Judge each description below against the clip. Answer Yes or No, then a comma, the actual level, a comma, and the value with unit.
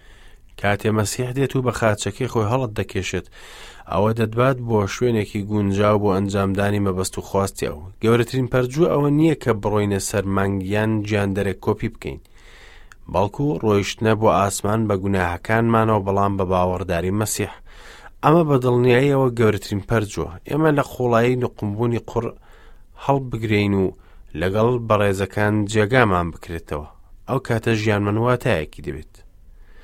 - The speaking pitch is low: Yes, low, 105 Hz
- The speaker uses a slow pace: Yes, slow, 120 wpm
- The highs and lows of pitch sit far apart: No, average, 3.5 semitones